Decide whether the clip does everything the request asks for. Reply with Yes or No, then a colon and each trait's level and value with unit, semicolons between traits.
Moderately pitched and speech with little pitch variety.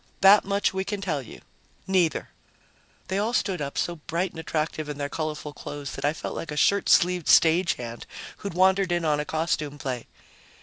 No: medium, 165 Hz; average, 4.2 semitones